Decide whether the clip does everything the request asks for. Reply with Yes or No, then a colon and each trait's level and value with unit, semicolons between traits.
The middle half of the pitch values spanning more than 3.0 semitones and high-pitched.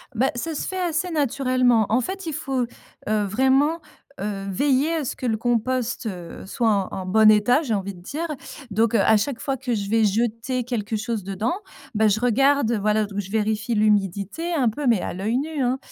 Yes: average, 4.2 semitones; high, 230 Hz